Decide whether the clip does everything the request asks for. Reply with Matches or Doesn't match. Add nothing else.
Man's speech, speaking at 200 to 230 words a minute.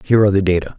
Doesn't match